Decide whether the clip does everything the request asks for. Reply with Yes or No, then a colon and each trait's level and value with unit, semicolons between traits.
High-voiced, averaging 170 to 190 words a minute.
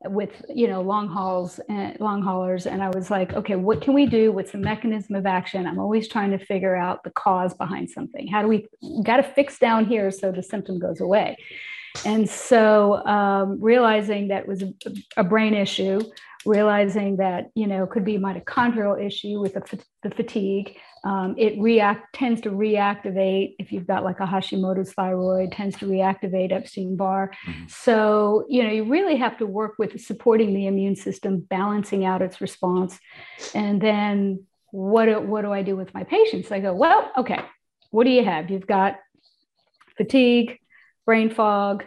Yes: high, 205 Hz; average, 185 wpm